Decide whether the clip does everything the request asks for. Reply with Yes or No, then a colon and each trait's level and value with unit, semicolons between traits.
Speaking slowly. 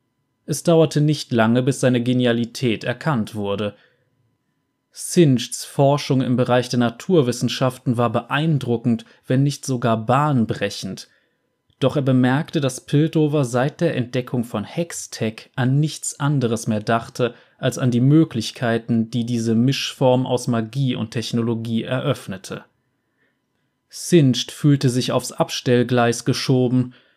Yes: slow, 120 wpm